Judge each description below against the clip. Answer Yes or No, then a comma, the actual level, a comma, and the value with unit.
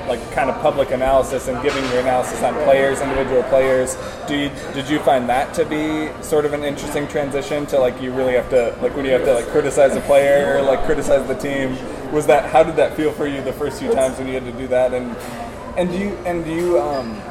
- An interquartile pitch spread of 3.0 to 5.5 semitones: No, narrow, 2.6 semitones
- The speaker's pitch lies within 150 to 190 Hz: No, medium, 140 Hz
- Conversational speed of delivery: No, fast, 240 wpm